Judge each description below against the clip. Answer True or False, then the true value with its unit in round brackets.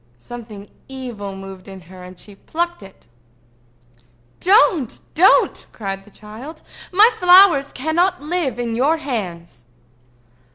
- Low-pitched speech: False (245 Hz)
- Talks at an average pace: False (120 wpm)